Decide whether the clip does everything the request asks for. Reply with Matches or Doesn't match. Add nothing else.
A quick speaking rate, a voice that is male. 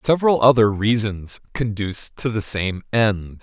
Doesn't match